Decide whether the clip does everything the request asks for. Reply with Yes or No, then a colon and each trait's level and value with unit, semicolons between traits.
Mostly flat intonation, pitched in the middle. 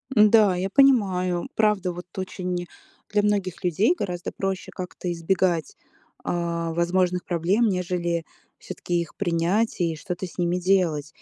Yes: narrow, 2.2 semitones; medium, 180 Hz